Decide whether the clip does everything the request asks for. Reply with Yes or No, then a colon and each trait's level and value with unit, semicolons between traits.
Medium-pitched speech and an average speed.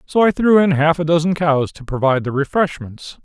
No: medium, 160 Hz; fast, 220 wpm